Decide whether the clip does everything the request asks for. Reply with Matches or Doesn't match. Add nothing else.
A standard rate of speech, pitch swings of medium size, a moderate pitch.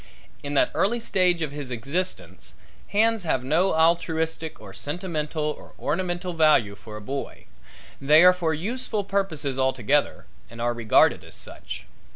Matches